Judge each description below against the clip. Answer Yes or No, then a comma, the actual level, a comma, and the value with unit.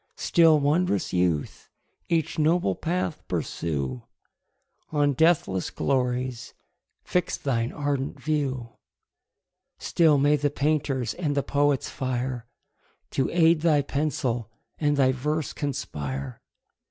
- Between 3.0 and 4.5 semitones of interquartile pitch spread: Yes, average, 3.9 semitones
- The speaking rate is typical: No, slow, 105 wpm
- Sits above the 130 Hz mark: Yes, medium, 140 Hz